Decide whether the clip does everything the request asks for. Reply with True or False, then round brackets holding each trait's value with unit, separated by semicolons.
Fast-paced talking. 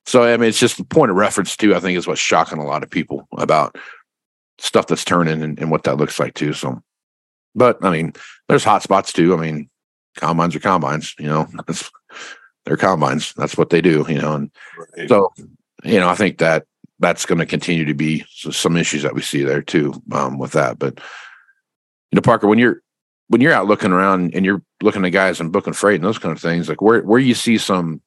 True (225 wpm)